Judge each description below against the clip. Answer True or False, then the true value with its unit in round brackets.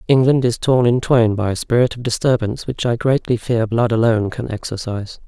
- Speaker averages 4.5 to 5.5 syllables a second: False (5.7 syllables/s)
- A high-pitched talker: False (115 Hz)